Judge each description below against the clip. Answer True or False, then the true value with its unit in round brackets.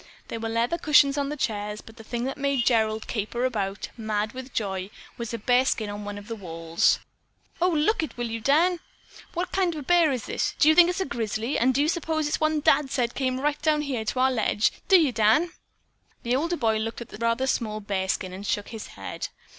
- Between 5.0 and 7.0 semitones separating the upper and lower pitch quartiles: True (5.5 semitones)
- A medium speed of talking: False (240 wpm)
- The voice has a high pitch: True (240 Hz)